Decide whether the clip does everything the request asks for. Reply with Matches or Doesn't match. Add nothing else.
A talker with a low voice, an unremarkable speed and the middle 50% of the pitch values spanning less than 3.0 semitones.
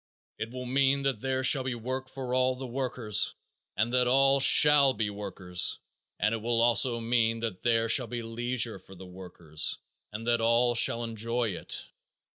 Matches